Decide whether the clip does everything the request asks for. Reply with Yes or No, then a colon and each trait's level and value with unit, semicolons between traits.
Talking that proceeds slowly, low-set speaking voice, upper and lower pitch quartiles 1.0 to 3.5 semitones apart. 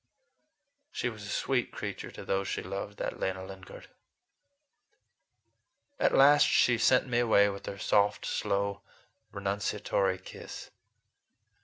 Yes: slow, 125 wpm; low, 100 Hz; average, 3.2 semitones